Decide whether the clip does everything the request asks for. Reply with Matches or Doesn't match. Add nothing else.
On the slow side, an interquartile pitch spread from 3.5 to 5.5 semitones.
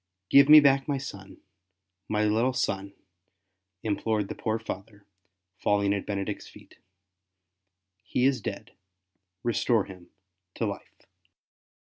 Matches